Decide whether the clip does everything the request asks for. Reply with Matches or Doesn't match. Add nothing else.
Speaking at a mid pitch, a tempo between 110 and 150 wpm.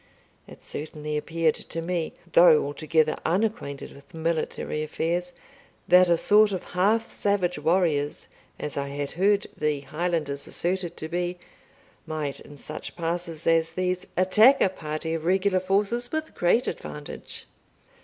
Matches